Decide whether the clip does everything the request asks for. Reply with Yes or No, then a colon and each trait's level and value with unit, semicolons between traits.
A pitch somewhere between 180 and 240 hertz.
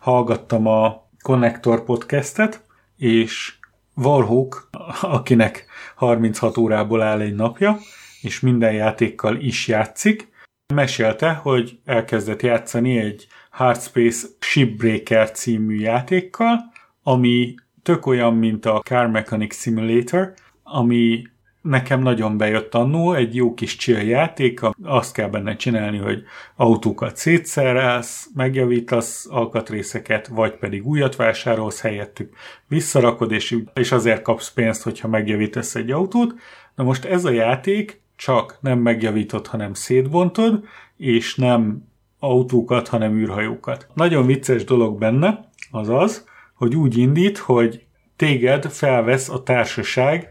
No: low, 120 Hz